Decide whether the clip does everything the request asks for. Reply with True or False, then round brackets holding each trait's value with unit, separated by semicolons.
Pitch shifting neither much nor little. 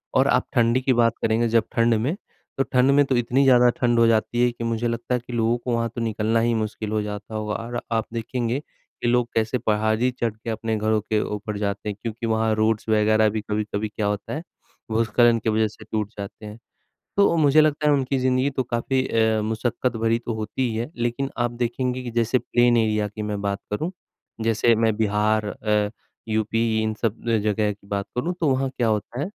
False (2.0 semitones)